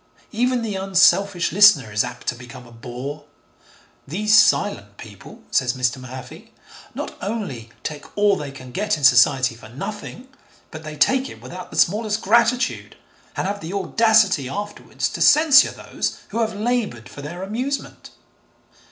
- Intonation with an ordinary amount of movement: No, wide, 8.8 semitones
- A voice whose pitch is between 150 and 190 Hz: Yes, medium, 185 Hz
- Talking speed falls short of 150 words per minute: No, average, 155 wpm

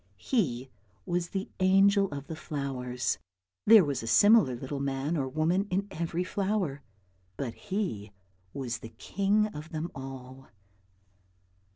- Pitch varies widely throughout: Yes, wide, 6.4 semitones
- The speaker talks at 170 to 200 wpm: No, slow, 135 wpm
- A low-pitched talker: No, medium, 155 Hz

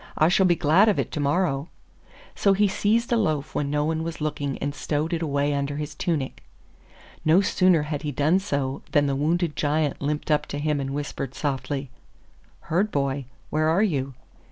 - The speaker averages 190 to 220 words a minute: Yes, average, 195 wpm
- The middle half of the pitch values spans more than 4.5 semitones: No, average, 3.1 semitones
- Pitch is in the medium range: Yes, medium, 150 Hz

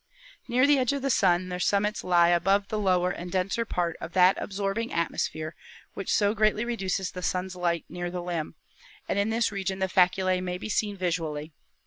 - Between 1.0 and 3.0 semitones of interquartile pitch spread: Yes, narrow, 2.6 semitones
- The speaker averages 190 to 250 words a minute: Yes, average, 195 wpm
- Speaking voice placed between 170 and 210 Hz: Yes, medium, 185 Hz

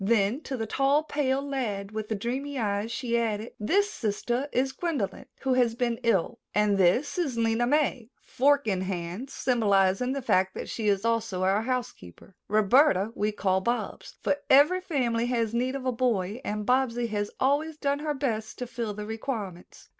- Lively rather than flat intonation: No, average, 4.3 semitones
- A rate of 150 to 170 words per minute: No, average, 180 wpm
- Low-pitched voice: No, high, 235 Hz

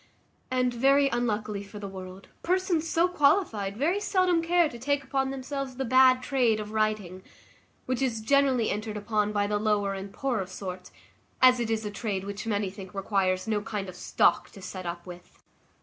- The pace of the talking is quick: No, average, 185 wpm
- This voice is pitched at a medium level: No, high, 220 Hz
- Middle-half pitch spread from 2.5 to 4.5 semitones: No, average, 5.1 semitones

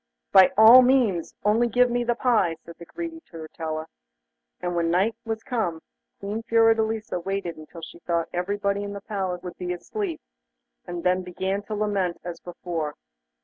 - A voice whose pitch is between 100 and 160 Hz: No, high, 195 Hz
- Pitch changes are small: No, average, 4.3 semitones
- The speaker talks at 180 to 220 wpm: No, average, 165 wpm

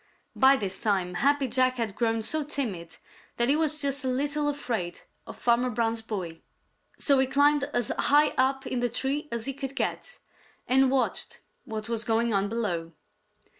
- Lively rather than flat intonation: No, average, 3.9 semitones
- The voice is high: Yes, very high, 250 Hz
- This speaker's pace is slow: No, average, 175 wpm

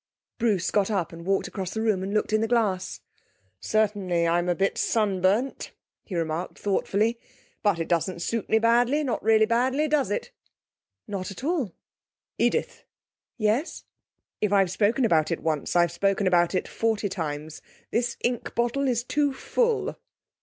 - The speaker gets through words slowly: No, average, 160 wpm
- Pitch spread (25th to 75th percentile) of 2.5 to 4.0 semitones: No, average, 4.4 semitones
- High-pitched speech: Yes, high, 205 Hz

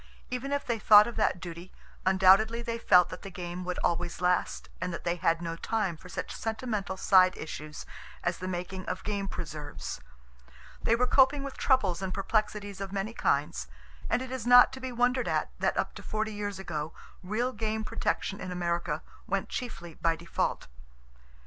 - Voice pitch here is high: Yes, high, 195 Hz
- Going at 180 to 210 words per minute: Yes, average, 185 wpm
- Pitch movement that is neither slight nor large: Yes, average, 4.5 semitones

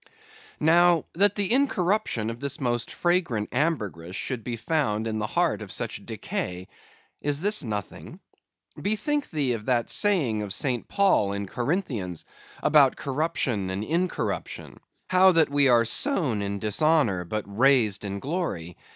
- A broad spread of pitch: Yes, wide, 8.0 semitones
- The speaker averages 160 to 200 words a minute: No, average, 145 wpm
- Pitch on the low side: Yes, low, 130 Hz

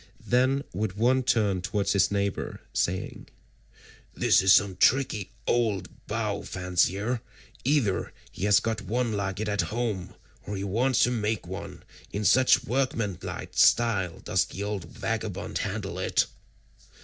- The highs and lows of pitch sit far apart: No, average, 3.7 semitones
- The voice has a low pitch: Yes, low, 105 Hz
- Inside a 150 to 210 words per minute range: No, average, 140 wpm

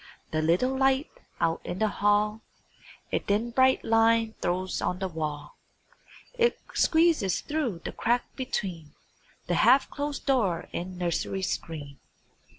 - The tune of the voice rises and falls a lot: Yes, wide, 6.9 semitones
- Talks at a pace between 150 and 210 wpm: No, slow, 135 wpm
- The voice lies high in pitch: Yes, high, 210 Hz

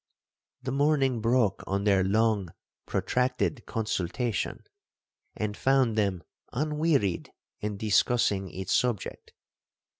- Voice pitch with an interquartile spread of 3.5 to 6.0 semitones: Yes, average, 4.5 semitones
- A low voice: Yes, low, 110 Hz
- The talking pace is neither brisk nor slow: No, slow, 95 wpm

